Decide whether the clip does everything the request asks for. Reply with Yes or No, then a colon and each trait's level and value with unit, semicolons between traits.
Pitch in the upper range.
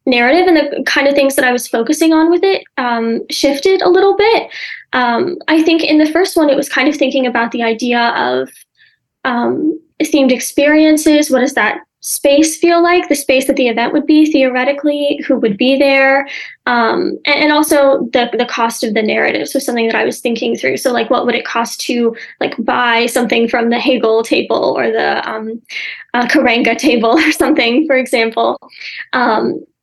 Yes: very high, 275 Hz